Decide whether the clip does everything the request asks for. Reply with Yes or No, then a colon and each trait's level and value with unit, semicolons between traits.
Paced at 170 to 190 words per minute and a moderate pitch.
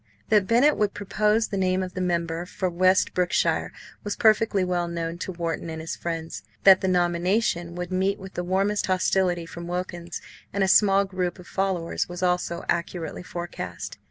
Yes: average, 180 wpm; medium, 180 Hz